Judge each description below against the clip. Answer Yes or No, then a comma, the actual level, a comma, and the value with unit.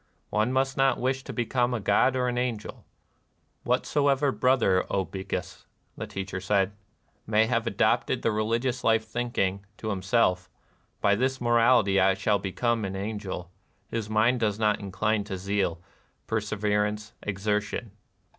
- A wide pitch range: No, average, 3.6 semitones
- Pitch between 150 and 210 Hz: No, low, 110 Hz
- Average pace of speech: Yes, average, 165 wpm